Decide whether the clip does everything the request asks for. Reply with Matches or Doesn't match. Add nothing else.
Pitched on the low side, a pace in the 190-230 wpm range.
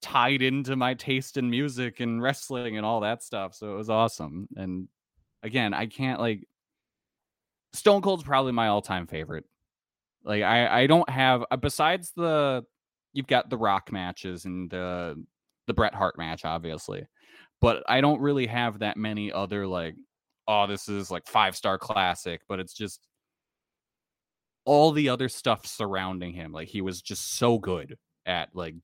Doesn't match